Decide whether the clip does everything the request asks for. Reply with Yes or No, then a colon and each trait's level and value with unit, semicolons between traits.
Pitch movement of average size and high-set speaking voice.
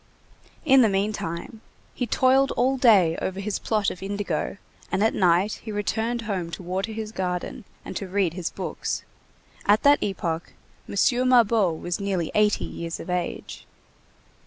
Yes: average, 3.7 semitones; high, 200 Hz